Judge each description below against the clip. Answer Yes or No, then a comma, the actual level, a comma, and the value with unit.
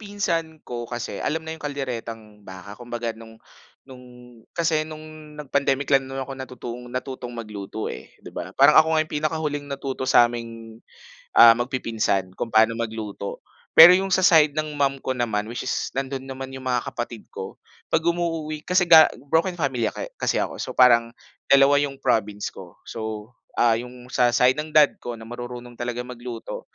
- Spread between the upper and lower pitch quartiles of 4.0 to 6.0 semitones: Yes, average, 4.5 semitones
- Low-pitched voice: Yes, low, 130 Hz